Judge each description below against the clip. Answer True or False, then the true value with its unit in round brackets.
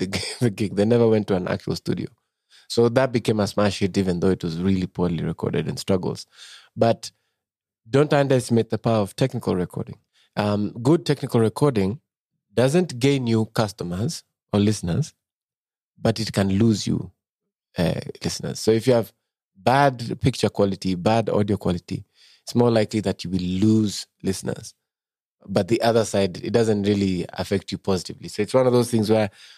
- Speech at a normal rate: False (170 wpm)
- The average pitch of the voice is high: False (110 Hz)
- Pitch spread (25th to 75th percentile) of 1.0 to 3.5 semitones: True (3.2 semitones)